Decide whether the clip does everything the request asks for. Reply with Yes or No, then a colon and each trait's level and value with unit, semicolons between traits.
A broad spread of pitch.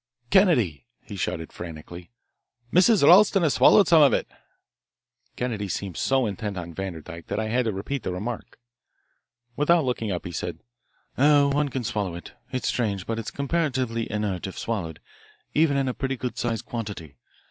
Yes: wide, 6.7 semitones